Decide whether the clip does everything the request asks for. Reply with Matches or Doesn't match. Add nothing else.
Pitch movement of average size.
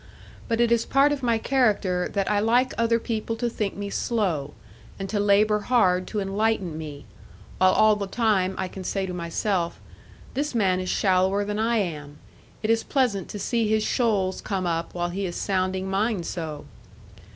Matches